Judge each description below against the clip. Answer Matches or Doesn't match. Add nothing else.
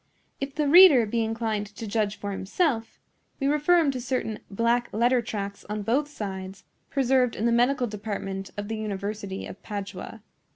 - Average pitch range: Matches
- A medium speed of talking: Matches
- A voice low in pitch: Doesn't match